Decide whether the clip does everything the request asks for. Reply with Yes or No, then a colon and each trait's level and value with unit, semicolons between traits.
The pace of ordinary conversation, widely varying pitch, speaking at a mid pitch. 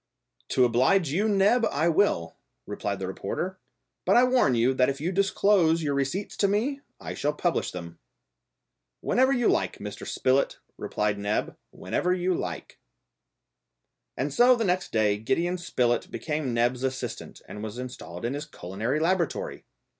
Yes: average, 155 wpm; wide, 8.0 semitones; medium, 145 Hz